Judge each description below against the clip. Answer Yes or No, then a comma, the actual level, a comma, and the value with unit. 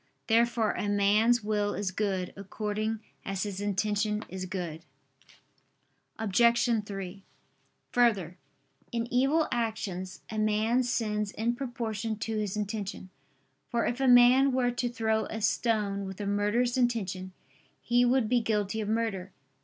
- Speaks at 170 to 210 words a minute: No, average, 140 wpm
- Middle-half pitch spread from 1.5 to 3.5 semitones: Yes, average, 2.9 semitones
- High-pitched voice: Yes, high, 215 Hz